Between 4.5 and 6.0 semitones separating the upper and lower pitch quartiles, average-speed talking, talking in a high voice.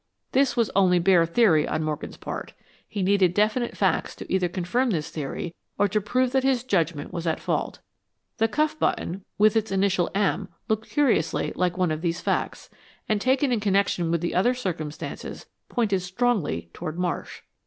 Yes: average, 5.1 semitones; average, 175 wpm; high, 195 Hz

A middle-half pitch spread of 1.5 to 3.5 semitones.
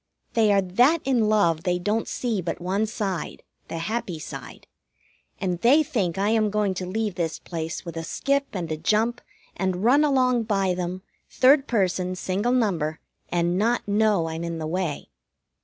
No: average, 4.3 semitones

